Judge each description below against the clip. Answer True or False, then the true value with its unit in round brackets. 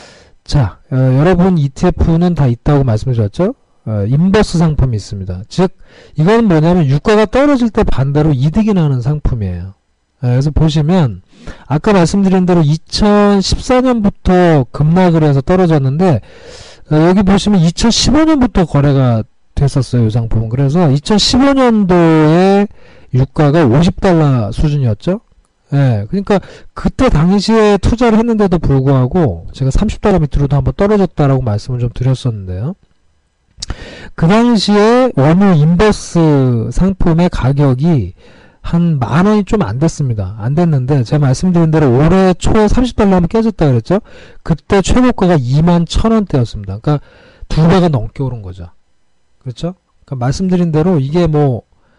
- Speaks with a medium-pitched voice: True (160 Hz)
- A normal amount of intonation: False (6.4 semitones)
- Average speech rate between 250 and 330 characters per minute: True (300 characters per minute)